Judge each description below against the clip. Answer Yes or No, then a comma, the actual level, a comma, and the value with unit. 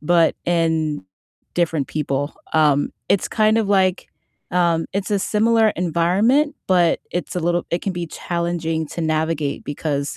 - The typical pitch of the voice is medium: Yes, medium, 170 Hz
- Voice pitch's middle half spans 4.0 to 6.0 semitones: No, average, 2.9 semitones